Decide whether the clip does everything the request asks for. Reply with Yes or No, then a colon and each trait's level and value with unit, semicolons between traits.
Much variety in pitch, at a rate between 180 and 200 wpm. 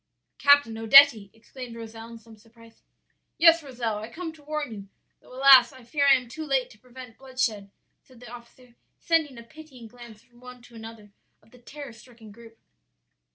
No: average, 3.2 semitones; average, 185 wpm